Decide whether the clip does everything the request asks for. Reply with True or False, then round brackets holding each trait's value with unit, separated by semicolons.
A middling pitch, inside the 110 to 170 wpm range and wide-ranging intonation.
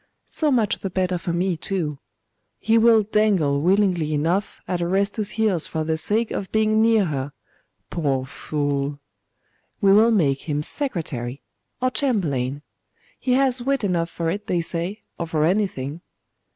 True (180 Hz; 150 wpm; 6.0 semitones)